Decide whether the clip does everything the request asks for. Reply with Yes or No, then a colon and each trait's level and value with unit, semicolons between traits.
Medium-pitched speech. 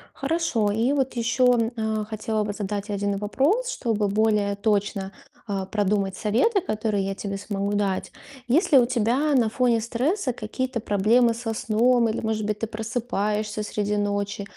No: high, 215 Hz